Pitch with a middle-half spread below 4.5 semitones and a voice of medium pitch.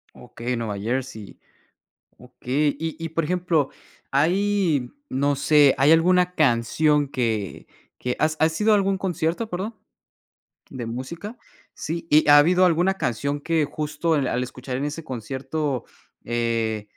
No: average, 4.8 semitones; medium, 150 Hz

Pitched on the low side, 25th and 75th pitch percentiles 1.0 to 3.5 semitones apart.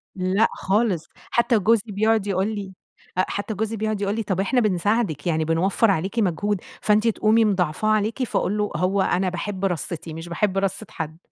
No: high, 200 Hz; average, 2.8 semitones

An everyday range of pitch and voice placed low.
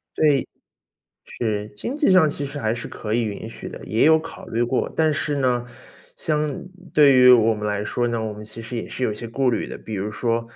Yes: average, 4.5 semitones; low, 120 Hz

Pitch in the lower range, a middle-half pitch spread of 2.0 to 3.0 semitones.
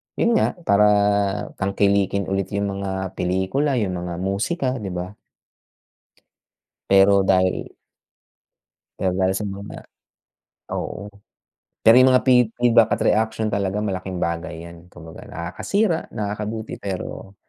Yes: low, 100 Hz; narrow, 2.6 semitones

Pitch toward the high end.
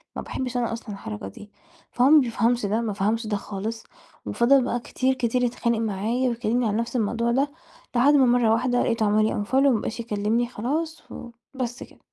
Yes: high, 235 Hz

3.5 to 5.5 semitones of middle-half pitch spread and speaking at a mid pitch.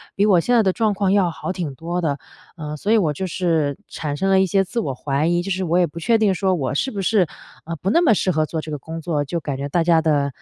Yes: average, 4.0 semitones; medium, 175 Hz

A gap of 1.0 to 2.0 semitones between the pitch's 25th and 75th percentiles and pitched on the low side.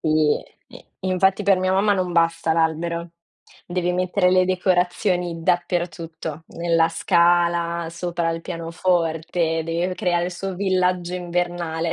No: narrow, 1.6 semitones; medium, 175 Hz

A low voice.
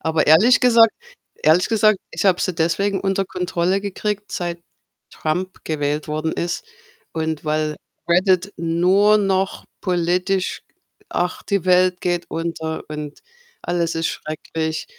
No: medium, 175 Hz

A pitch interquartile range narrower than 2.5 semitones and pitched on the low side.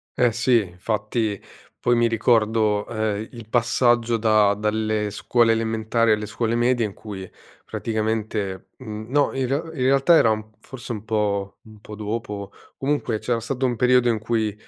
Yes: narrow, 2.0 semitones; low, 110 Hz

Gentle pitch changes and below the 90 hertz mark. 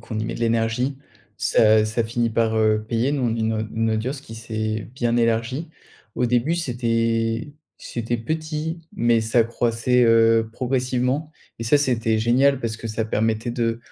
No: narrow, 1.9 semitones; low, 115 Hz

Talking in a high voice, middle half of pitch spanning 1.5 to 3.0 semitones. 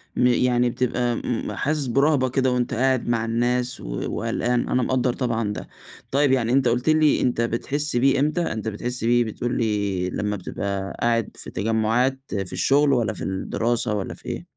No: low, 120 Hz; narrow, 2.6 semitones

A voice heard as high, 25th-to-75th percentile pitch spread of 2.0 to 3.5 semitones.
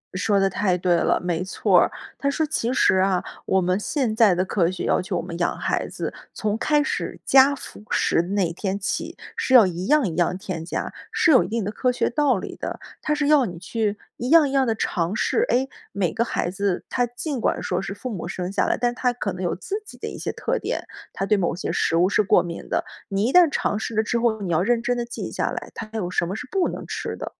No: high, 210 Hz; wide, 5.4 semitones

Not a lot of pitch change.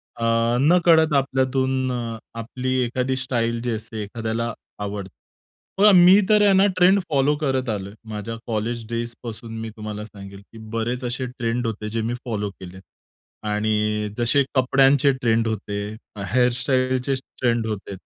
No: average, 3.1 semitones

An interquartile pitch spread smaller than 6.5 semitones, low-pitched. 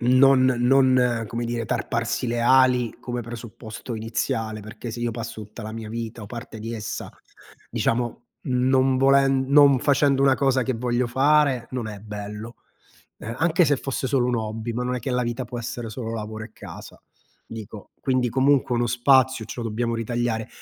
Yes: narrow, 2.5 semitones; low, 120 Hz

